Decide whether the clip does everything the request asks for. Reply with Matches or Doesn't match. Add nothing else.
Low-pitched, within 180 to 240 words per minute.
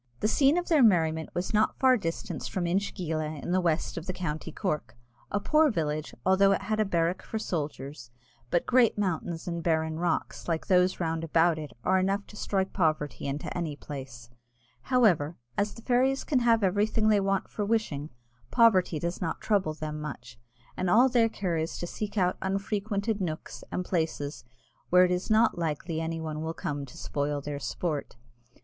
Doesn't match